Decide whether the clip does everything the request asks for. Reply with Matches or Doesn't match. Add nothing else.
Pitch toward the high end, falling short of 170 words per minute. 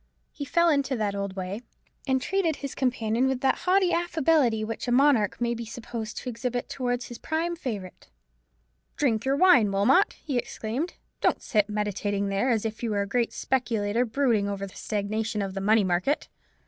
Doesn't match